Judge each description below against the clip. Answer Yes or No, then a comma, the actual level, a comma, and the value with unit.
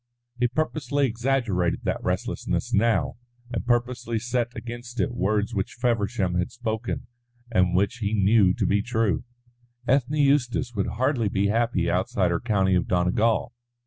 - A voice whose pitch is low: Yes, low, 115 Hz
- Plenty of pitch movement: No, average, 3.8 semitones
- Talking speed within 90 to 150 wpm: Yes, average, 145 wpm